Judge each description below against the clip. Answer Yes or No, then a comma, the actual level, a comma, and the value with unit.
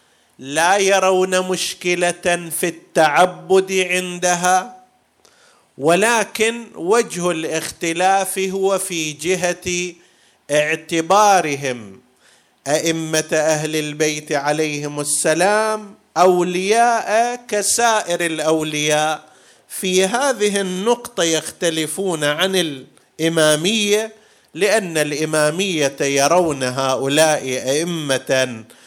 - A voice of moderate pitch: Yes, medium, 175 Hz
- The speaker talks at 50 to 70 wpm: Yes, slow, 65 wpm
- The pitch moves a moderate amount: Yes, average, 3.9 semitones